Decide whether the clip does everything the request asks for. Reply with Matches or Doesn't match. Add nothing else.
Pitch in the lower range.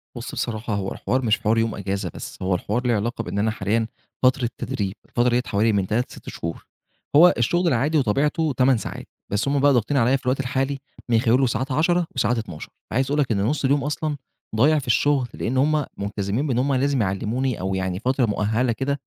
Matches